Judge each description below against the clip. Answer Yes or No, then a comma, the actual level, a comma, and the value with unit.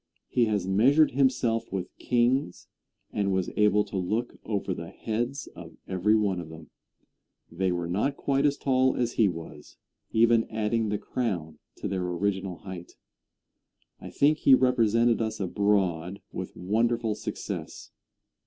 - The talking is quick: No, average, 145 wpm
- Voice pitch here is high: No, low, 105 Hz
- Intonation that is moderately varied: Yes, average, 4.3 semitones